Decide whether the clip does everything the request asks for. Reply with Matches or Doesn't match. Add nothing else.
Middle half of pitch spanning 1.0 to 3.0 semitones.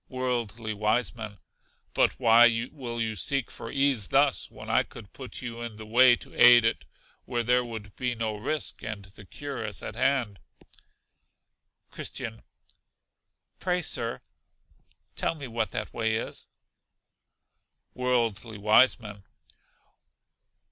Matches